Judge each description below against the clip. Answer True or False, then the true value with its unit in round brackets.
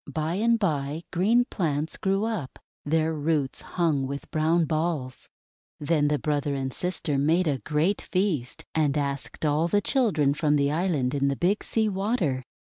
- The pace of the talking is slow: False (165 wpm)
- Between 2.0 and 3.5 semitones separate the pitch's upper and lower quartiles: False (4.2 semitones)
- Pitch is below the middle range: False (155 Hz)